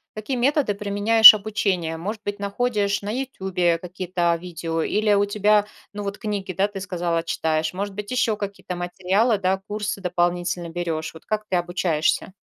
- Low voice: No, high, 195 Hz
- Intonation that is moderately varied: Yes, average, 3.0 semitones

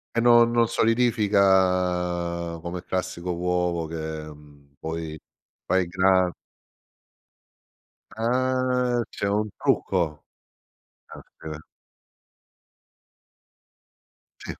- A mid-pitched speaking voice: No, very low, 90 Hz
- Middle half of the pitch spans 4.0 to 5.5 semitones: Yes, average, 4.9 semitones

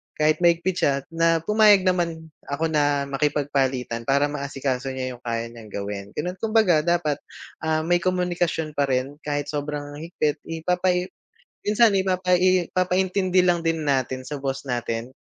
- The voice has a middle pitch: Yes, medium, 155 Hz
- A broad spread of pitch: No, average, 4.6 semitones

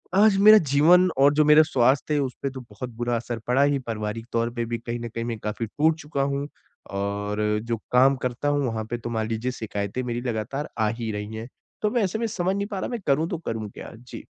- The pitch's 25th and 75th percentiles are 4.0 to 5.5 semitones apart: Yes, average, 4.5 semitones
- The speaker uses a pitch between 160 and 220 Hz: No, low, 125 Hz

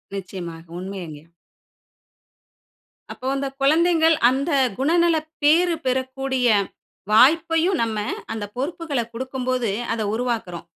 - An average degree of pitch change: No, wide, 6.7 semitones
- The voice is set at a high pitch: Yes, very high, 260 Hz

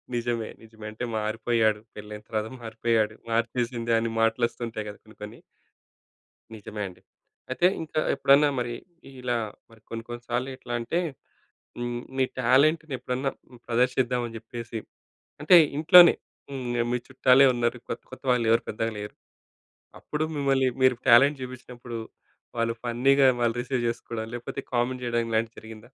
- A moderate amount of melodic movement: No, narrow, 2.2 semitones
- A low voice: Yes, low, 120 Hz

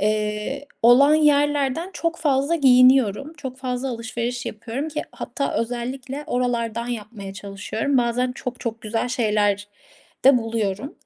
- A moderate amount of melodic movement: Yes, average, 3.6 semitones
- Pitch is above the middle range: Yes, high, 245 Hz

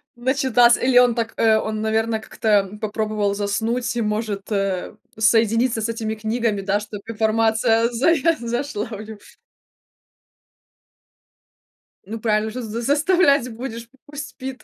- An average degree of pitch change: No, narrow, 2.1 semitones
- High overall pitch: Yes, high, 225 Hz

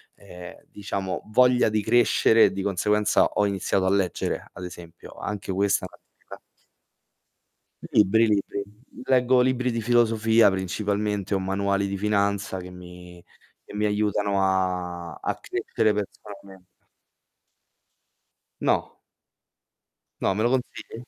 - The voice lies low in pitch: Yes, low, 100 Hz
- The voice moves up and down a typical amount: No, narrow, 2.2 semitones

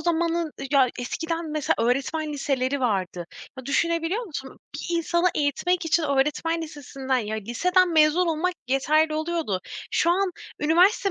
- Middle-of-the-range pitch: No, very high, 310 Hz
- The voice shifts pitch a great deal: No, average, 4.0 semitones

